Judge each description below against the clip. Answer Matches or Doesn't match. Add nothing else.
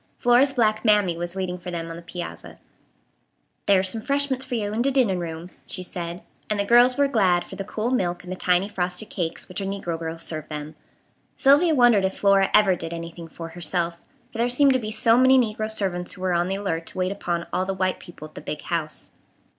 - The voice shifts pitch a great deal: Doesn't match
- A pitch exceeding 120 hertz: Matches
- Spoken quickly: Matches